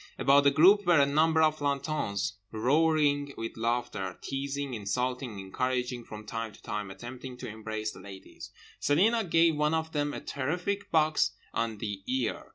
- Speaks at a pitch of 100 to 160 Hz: Yes, low, 135 Hz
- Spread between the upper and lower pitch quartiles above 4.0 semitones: Yes, wide, 5.4 semitones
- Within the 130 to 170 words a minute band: Yes, average, 165 wpm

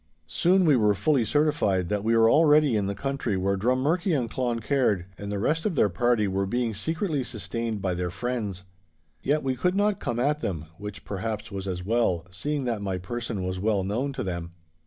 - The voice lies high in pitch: No, low, 115 Hz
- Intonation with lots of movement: Yes, wide, 5.9 semitones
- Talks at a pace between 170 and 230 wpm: Yes, average, 200 wpm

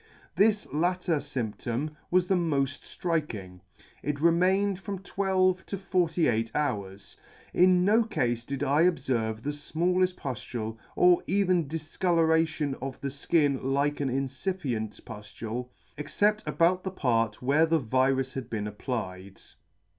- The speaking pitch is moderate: Yes, medium, 145 Hz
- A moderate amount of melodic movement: No, wide, 6.3 semitones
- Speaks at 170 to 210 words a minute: No, slow, 135 wpm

